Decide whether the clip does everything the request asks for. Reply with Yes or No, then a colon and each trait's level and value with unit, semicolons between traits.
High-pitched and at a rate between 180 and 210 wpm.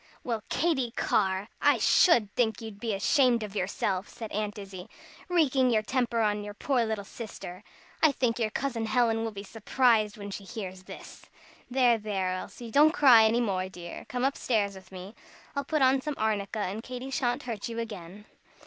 Yes: high, 220 Hz; average, 185 wpm